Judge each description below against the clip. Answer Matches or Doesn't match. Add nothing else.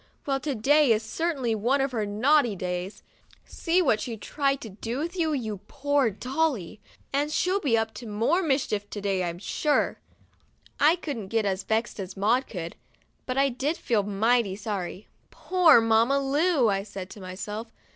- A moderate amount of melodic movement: Doesn't match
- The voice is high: Matches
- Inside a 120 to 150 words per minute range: Doesn't match